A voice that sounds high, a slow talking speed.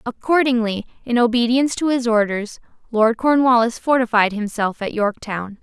Yes: high, 235 Hz; slow, 130 wpm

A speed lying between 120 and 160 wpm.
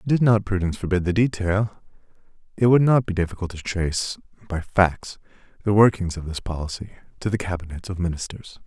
No: average, 175 wpm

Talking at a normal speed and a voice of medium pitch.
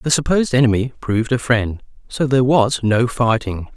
No: average, 175 wpm; low, 120 Hz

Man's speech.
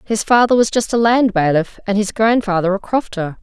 No: female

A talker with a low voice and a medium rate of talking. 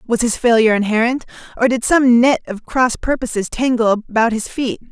No: high, 235 Hz; average, 185 wpm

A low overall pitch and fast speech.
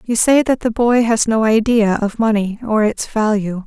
No: high, 220 Hz; fast, 215 wpm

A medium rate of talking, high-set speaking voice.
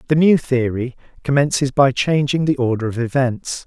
No: average, 165 wpm; low, 135 Hz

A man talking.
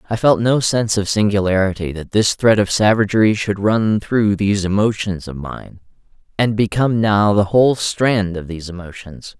Yes: male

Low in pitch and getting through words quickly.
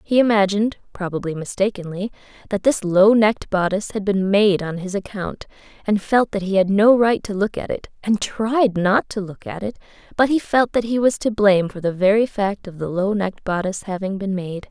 No: high, 200 Hz; fast, 215 wpm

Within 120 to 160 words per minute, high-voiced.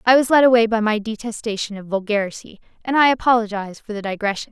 No: average, 200 wpm; high, 220 Hz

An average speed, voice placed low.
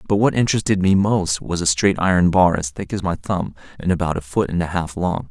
No: fast, 260 wpm; very low, 90 Hz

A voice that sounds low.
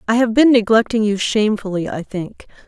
No: high, 215 Hz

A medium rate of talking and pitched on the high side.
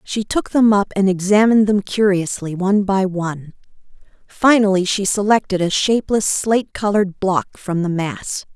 Yes: average, 155 wpm; high, 195 Hz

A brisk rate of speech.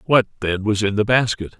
Yes: fast, 225 wpm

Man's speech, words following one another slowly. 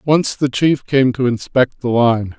No: male; average, 200 wpm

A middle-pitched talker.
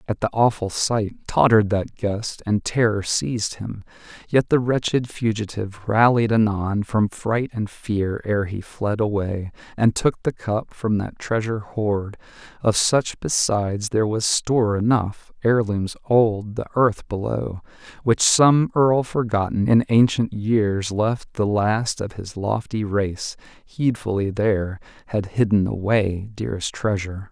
No: low, 110 Hz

